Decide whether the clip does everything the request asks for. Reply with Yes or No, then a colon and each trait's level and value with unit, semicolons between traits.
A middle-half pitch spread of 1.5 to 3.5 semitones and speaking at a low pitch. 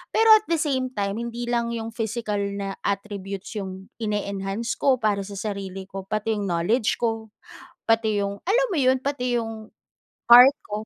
No: average, 3.2 semitones; high, 220 Hz